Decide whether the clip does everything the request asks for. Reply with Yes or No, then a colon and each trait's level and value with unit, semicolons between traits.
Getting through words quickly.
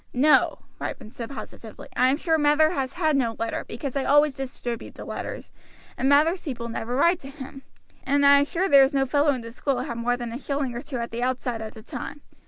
Yes: fast, 235 wpm